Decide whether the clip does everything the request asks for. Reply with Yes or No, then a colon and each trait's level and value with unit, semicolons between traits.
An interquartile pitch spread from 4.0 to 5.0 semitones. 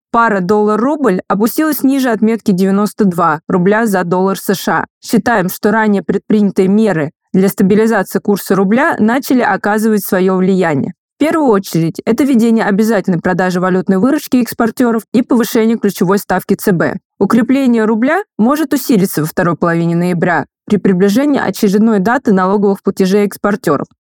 No: average, 3.1 semitones